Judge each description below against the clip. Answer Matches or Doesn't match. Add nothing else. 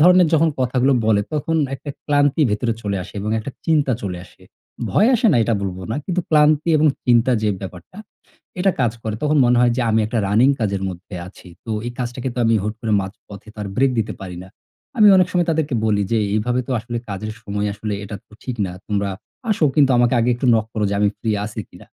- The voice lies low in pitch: Matches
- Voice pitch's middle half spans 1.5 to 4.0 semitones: Doesn't match